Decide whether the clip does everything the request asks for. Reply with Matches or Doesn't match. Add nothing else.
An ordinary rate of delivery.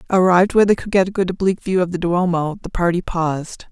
Doesn't match